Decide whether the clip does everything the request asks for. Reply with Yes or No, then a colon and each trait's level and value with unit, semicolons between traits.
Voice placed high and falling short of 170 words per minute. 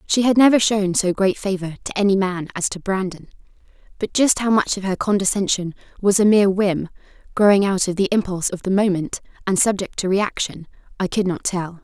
No: high, 195 Hz; fast, 205 wpm